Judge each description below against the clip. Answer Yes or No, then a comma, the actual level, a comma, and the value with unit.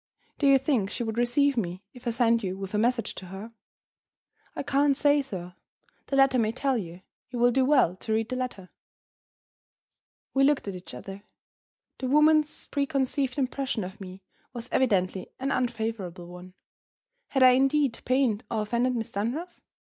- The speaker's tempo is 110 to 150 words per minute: No, average, 170 wpm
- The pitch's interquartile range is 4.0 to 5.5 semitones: Yes, average, 5.2 semitones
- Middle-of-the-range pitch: No, high, 240 Hz